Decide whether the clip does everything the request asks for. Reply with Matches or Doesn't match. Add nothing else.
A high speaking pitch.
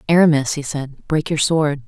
Doesn't match